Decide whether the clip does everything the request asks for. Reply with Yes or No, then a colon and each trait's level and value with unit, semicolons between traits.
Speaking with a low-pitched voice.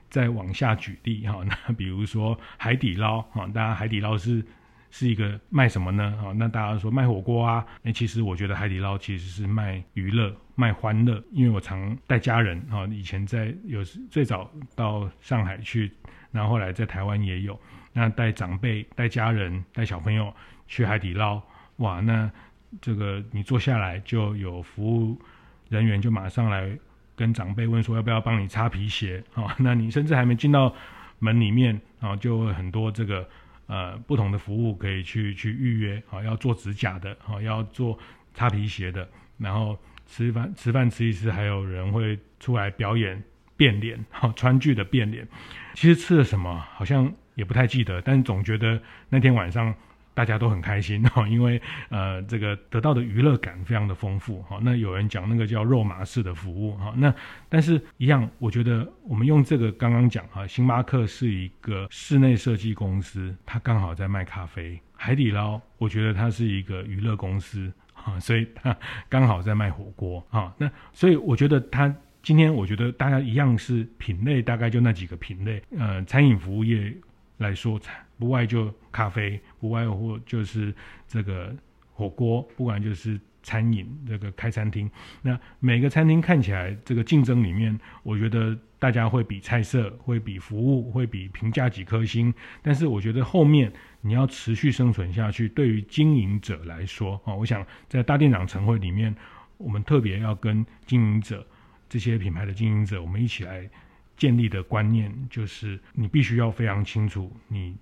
Yes: low, 110 Hz